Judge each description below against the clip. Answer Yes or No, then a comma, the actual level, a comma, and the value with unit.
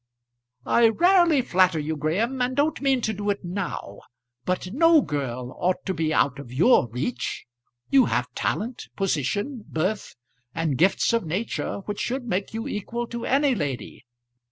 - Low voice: No, high, 195 Hz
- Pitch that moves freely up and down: Yes, wide, 7.8 semitones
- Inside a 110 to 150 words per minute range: No, average, 160 wpm